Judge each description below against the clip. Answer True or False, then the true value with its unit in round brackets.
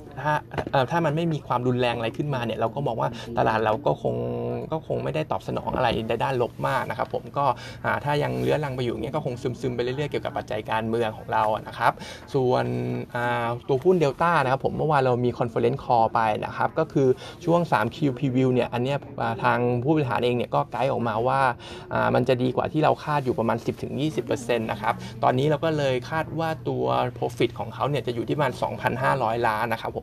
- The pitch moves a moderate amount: True (3.6 semitones)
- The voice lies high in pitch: False (125 Hz)